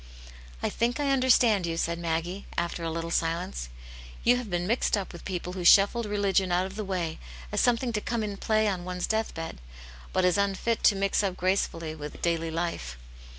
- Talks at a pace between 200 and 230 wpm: Yes, fast, 205 wpm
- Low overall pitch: No, medium, 185 Hz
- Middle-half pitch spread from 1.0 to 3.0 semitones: No, average, 4.0 semitones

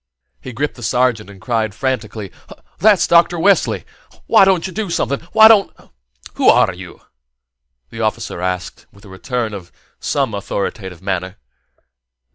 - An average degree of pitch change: No, wide, 8.4 semitones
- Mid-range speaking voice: No, low, 115 Hz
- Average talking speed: Yes, average, 150 wpm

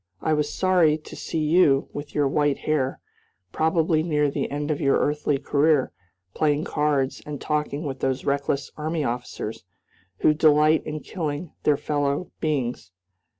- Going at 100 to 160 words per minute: Yes, average, 150 wpm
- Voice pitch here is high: No, medium, 150 Hz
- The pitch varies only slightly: Yes, narrow, 1.7 semitones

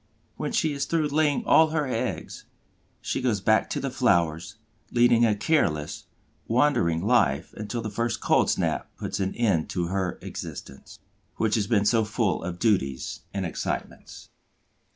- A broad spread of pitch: Yes, wide, 5.8 semitones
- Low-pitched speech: Yes, low, 110 Hz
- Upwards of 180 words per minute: No, average, 155 wpm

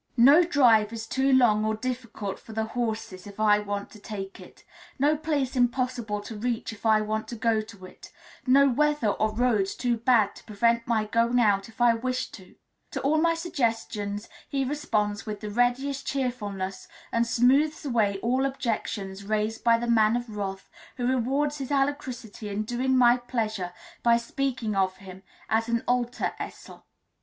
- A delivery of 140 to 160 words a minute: No, average, 175 wpm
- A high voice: Yes, high, 230 Hz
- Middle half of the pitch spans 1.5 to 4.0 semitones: Yes, average, 3.2 semitones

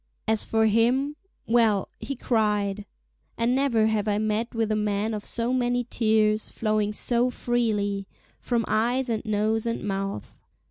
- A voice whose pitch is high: Yes, high, 220 Hz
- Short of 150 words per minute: Yes, average, 140 wpm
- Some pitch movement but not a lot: No, narrow, 2.1 semitones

